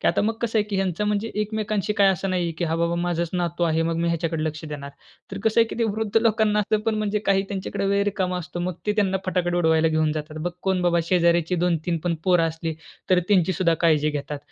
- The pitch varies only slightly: No, average, 3.6 semitones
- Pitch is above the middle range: No, medium, 180 Hz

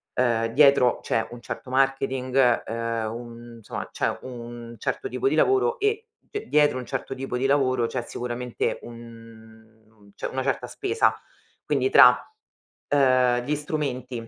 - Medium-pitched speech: No, low, 125 Hz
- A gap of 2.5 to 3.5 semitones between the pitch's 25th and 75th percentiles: Yes, average, 2.8 semitones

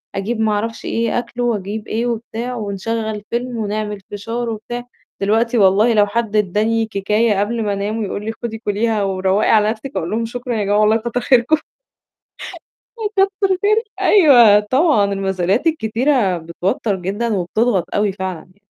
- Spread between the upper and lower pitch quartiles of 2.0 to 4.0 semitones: Yes, average, 2.7 semitones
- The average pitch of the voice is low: No, high, 220 Hz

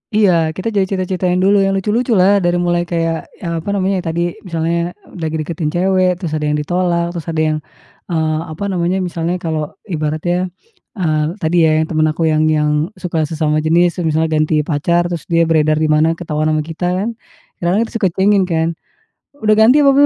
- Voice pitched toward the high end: No, medium, 170 Hz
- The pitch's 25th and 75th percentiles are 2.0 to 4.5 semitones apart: Yes, average, 2.7 semitones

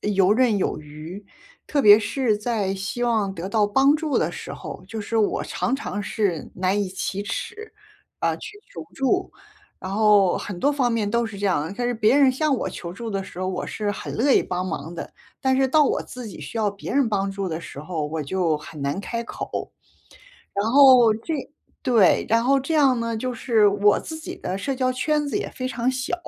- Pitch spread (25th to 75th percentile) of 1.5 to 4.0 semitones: No, average, 4.9 semitones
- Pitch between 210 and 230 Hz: Yes, high, 220 Hz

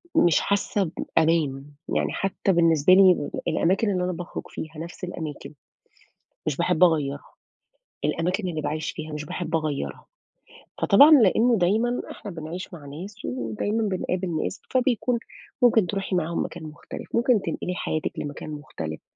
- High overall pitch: No, medium, 175 Hz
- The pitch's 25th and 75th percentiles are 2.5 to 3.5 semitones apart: No, average, 4.2 semitones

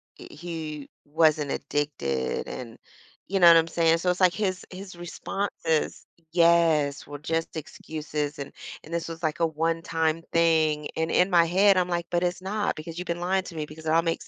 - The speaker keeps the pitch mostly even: Yes, narrow, 2.3 semitones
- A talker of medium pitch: Yes, medium, 165 Hz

